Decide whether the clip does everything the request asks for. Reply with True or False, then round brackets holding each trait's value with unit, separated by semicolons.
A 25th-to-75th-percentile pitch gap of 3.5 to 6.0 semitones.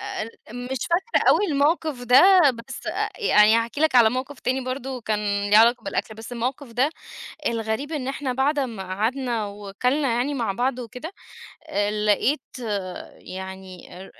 True (3.9 semitones)